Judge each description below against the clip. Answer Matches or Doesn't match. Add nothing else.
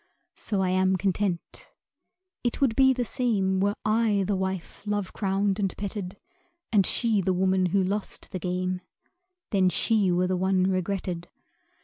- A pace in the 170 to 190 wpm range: Doesn't match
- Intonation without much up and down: Matches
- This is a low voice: Doesn't match